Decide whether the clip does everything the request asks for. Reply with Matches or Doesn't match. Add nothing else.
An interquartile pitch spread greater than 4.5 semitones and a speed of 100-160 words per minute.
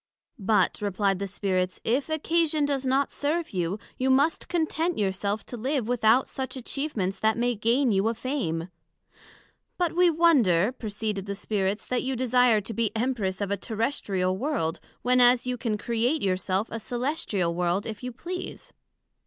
Doesn't match